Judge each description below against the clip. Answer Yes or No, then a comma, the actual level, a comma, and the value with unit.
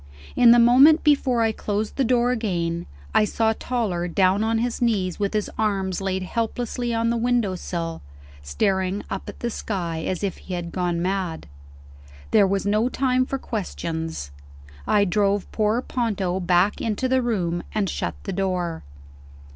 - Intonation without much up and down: No, average, 4.3 semitones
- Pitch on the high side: Yes, high, 205 Hz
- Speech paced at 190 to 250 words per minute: No, average, 165 wpm